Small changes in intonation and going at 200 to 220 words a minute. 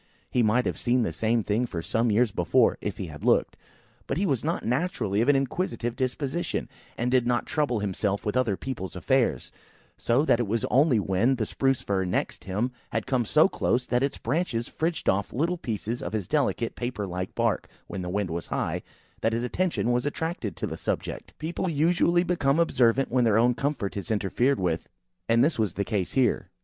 No: average, 4.8 semitones; fast, 205 wpm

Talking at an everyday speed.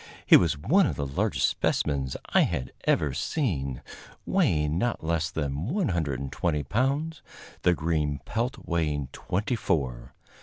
No: slow, 130 wpm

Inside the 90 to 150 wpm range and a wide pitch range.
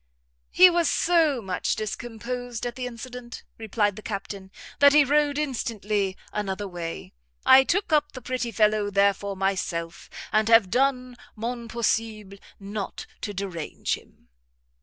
No: average, 140 wpm; average, 4.1 semitones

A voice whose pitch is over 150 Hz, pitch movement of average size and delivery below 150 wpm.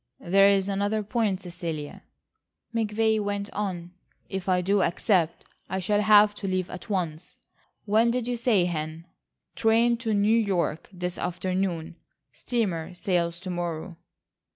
Yes: high, 190 Hz; average, 3.3 semitones; slow, 135 wpm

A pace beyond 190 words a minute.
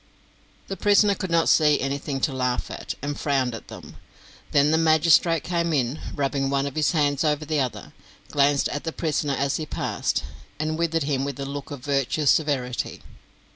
No: average, 185 wpm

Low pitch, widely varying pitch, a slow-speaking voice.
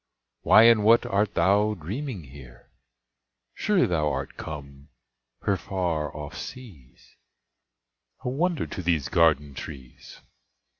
Yes: very low, 85 Hz; wide, 6.8 semitones; slow, 115 wpm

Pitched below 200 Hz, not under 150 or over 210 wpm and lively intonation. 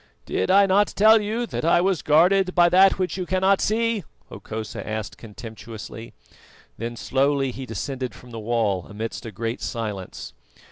Yes: low, 135 Hz; average, 160 wpm; wide, 9.0 semitones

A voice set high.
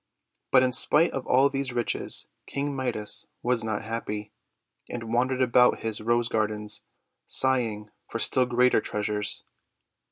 No: low, 120 Hz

